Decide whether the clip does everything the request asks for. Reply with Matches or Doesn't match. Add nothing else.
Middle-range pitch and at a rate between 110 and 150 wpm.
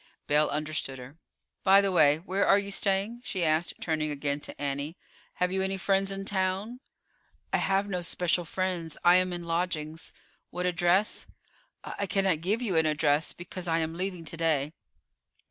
Doesn't match